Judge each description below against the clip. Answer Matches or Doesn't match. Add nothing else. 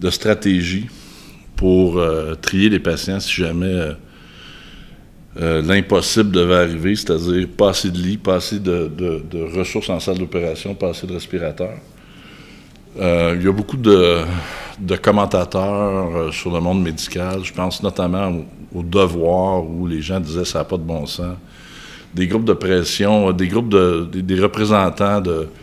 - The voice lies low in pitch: Matches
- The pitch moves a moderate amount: Doesn't match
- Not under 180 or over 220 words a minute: Doesn't match